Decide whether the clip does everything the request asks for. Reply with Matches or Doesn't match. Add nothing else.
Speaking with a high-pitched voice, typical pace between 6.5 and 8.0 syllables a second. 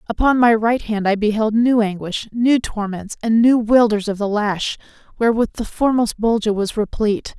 Doesn't match